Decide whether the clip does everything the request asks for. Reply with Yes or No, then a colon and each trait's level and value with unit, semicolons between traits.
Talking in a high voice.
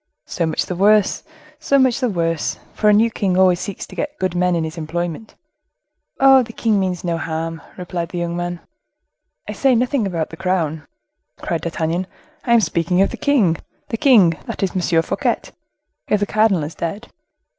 No: medium, 180 Hz